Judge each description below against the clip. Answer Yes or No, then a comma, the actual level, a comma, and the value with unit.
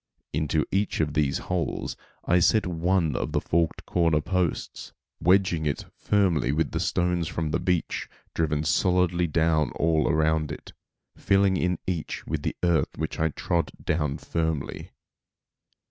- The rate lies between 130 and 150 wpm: Yes, average, 140 wpm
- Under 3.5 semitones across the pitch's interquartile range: Yes, narrow, 2.6 semitones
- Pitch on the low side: Yes, very low, 80 Hz